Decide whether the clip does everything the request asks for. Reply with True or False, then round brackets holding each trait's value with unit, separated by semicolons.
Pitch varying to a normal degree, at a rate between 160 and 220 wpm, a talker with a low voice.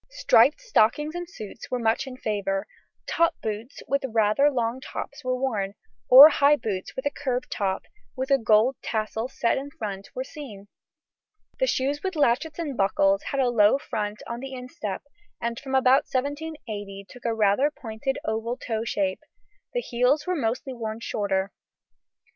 False (4.6 semitones; 170 wpm; 245 Hz)